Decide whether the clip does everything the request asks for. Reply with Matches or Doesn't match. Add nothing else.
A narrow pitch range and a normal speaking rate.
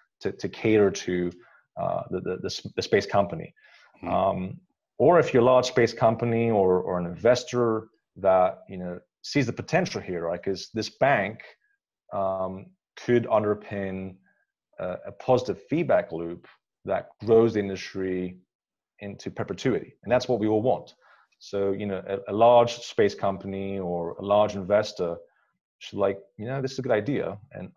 Doesn't match